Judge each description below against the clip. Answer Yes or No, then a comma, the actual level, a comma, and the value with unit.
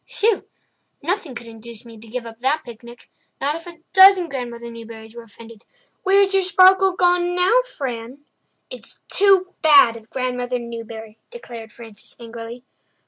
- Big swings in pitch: Yes, wide, 7.7 semitones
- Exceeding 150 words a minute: No, average, 145 wpm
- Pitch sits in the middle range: No, very high, 250 Hz